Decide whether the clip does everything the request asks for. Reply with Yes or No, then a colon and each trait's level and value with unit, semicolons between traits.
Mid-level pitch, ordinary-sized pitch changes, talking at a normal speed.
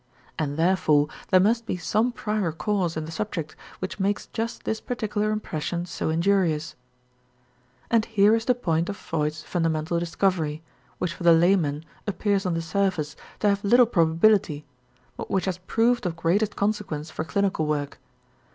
Yes: medium, 180 Hz; average, 4.5 semitones; average, 160 wpm